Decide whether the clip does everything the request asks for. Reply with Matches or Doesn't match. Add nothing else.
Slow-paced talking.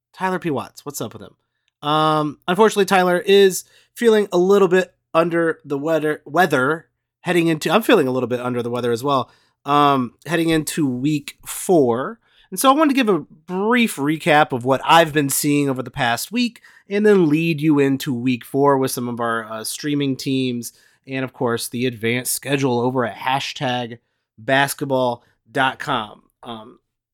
Doesn't match